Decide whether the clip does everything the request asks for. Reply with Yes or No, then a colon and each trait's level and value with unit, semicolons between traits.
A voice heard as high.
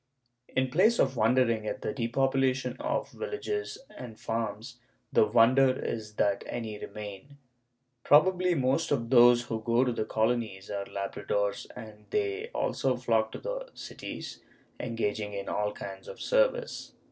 No: low, 120 Hz